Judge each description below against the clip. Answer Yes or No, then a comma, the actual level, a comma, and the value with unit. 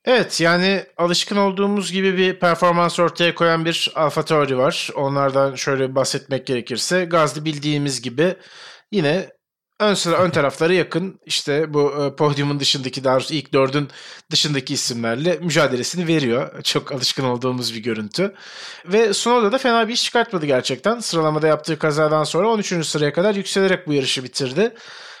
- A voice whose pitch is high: No, medium, 155 Hz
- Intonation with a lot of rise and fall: No, average, 4.7 semitones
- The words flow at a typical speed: No, fast, 145 wpm